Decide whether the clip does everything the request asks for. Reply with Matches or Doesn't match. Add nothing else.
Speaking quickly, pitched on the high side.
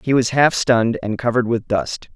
Doesn't match